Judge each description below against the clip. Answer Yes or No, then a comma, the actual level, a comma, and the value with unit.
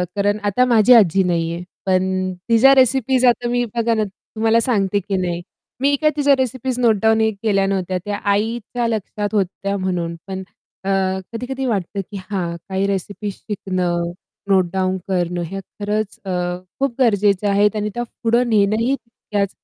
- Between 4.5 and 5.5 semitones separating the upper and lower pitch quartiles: No, average, 3.6 semitones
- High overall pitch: Yes, high, 205 Hz